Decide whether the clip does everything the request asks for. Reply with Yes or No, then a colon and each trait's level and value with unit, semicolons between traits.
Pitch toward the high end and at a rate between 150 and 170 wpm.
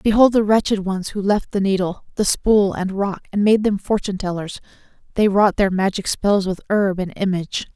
No: high, 200 Hz; average, 200 wpm